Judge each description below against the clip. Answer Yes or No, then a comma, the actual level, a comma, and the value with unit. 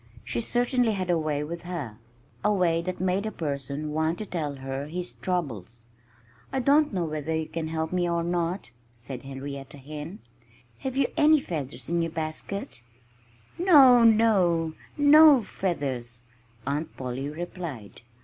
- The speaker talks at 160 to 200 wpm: No, average, 150 wpm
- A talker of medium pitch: Yes, medium, 165 Hz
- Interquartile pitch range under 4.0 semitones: No, wide, 5.4 semitones